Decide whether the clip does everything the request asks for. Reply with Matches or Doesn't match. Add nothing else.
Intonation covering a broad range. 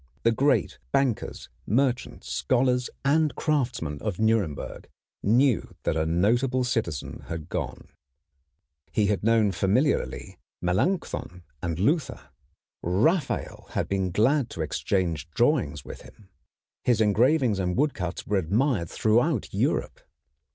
Matches